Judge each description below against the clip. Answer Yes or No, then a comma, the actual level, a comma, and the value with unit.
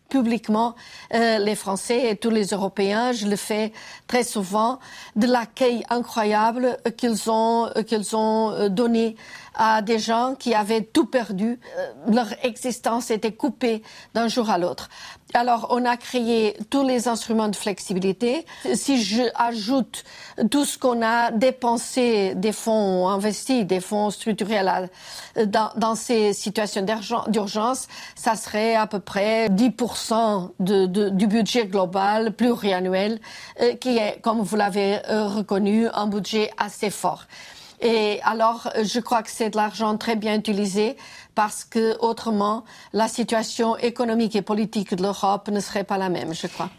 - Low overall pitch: No, high, 225 Hz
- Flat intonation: Yes, narrow, 2.2 semitones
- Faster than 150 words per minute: No, slow, 145 wpm